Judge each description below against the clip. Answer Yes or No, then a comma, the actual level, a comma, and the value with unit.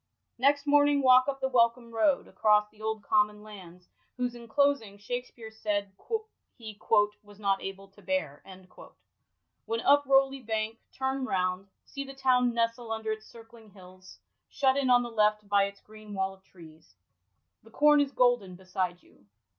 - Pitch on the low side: No, high, 220 Hz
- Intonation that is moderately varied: Yes, average, 4.3 semitones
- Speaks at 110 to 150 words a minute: No, average, 170 wpm